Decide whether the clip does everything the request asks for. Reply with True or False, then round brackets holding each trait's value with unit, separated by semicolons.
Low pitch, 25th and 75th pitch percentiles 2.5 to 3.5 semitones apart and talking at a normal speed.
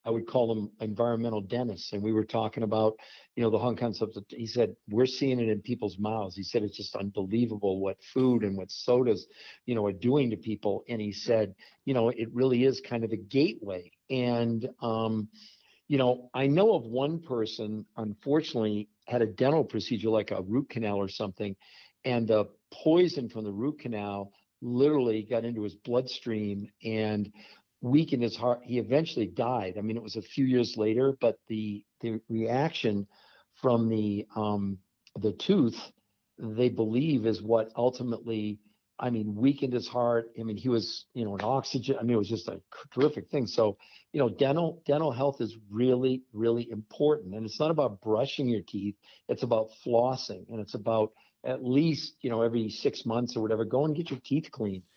True (115 Hz; 2.9 semitones; 190 wpm)